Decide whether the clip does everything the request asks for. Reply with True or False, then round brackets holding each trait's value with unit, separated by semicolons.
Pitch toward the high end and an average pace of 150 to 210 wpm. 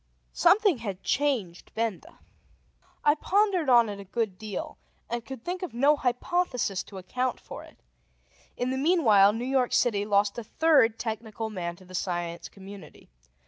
True (230 Hz; 160 wpm)